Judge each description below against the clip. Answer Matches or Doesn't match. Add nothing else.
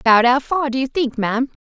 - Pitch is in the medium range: Doesn't match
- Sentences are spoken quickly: Matches